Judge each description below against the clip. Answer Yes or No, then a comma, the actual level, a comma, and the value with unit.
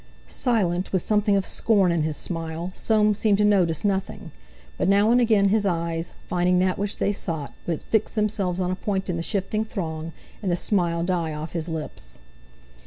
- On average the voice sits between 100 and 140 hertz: No, medium, 185 Hz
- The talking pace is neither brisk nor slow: Yes, average, 190 wpm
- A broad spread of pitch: No, average, 3.5 semitones